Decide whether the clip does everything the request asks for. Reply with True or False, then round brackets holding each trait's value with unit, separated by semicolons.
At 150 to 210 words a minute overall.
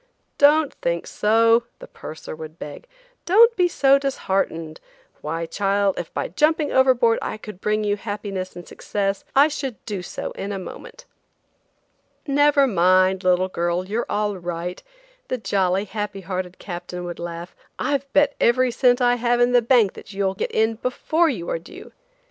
True (165 wpm)